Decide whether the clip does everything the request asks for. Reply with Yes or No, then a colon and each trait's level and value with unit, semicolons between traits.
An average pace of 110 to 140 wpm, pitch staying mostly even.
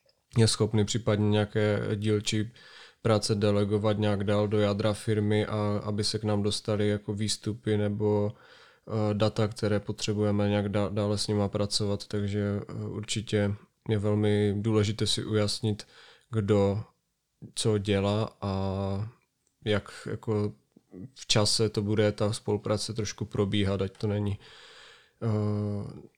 Yes: average, 120 wpm; narrow, 0.8 semitones